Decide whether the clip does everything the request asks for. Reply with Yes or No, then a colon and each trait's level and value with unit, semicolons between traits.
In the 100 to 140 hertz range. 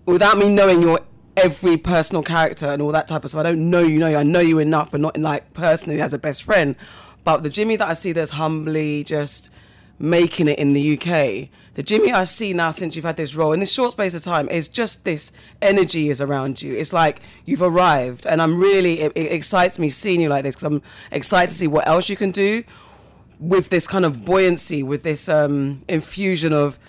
No: medium, 160 Hz